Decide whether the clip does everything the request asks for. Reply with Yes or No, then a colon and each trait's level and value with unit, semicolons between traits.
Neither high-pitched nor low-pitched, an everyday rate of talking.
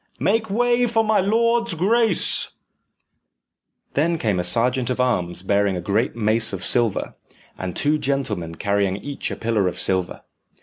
No: low, 120 Hz; average, 150 wpm